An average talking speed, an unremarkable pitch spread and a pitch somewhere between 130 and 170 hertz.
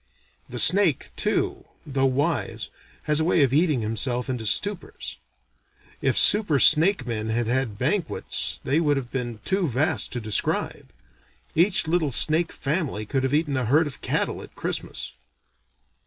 Yes: average, 155 wpm; average, 4.9 semitones; medium, 140 Hz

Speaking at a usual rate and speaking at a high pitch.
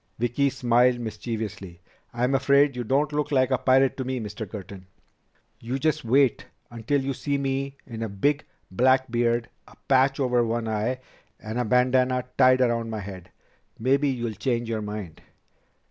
No: average, 165 wpm; low, 125 Hz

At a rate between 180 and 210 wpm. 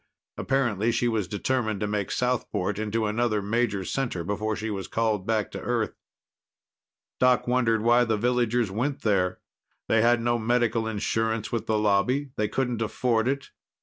No: average, 160 wpm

